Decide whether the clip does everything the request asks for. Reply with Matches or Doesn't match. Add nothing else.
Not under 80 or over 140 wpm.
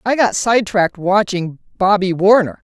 Matches